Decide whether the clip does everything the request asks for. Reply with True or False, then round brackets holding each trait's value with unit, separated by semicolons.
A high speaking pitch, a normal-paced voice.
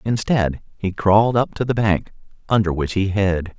False (100 Hz; 185 wpm)